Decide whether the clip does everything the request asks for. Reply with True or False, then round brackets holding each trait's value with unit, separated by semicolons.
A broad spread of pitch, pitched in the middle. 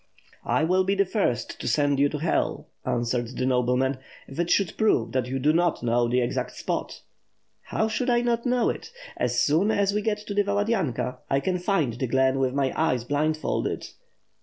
True (7.8 semitones; 150 Hz)